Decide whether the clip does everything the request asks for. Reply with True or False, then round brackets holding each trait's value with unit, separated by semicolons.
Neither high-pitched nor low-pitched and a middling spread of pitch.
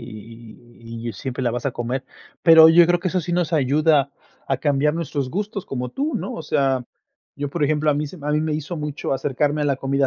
True (145 Hz; 3.8 semitones)